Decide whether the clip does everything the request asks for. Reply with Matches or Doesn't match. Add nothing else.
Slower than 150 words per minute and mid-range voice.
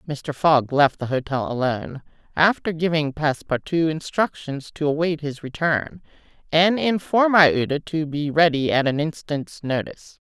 Matches